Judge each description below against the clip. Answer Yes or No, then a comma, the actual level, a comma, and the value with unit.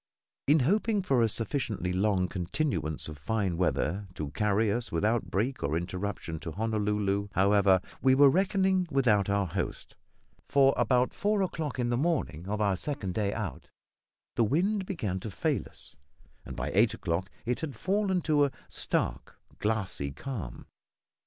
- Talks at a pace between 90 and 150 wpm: No, average, 160 wpm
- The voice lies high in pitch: No, low, 110 Hz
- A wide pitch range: Yes, wide, 6.8 semitones